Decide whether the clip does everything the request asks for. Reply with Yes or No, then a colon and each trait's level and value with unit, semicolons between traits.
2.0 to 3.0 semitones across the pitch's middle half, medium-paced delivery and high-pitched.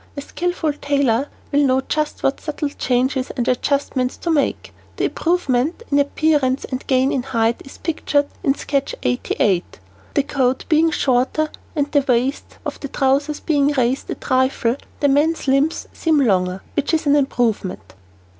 Yes: narrow, 2.4 semitones; average, 160 wpm; very high, 275 Hz